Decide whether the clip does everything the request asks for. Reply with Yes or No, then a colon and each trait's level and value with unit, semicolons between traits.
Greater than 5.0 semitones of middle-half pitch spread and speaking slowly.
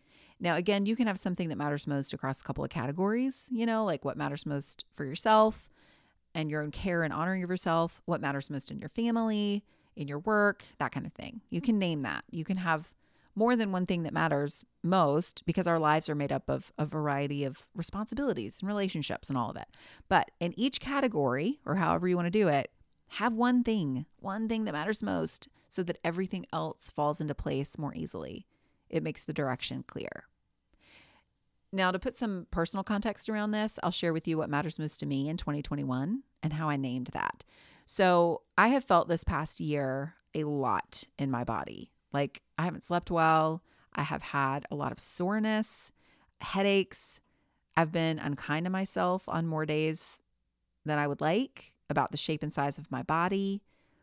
No: wide, 5.5 semitones; average, 195 wpm